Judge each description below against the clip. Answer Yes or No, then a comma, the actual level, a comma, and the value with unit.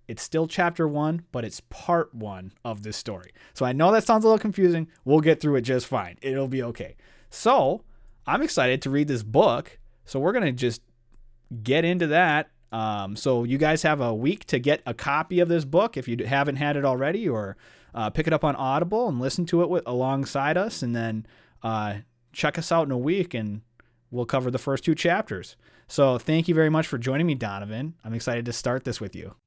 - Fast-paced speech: Yes, fast, 220 wpm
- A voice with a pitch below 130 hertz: No, low, 135 Hz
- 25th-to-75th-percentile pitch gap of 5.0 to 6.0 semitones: Yes, average, 5.3 semitones